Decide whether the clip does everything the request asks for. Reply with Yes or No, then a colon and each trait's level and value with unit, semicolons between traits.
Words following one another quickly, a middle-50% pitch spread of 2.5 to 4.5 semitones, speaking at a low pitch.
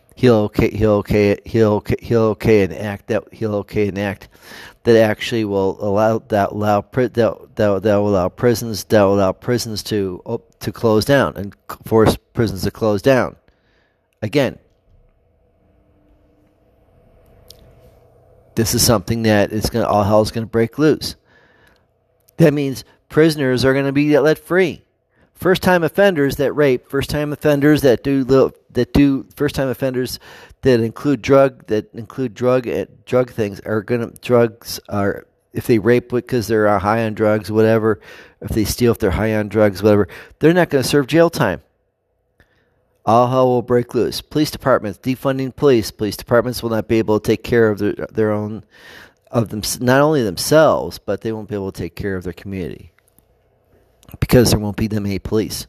No: average, 170 wpm; average, 3.6 semitones; low, 115 Hz